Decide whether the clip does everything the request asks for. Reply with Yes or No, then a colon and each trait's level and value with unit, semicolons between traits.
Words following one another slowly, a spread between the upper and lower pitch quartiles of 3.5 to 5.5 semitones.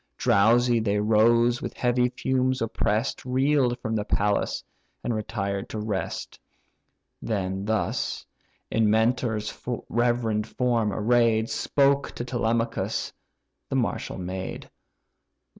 No: slow, 110 wpm; narrow, 2.4 semitones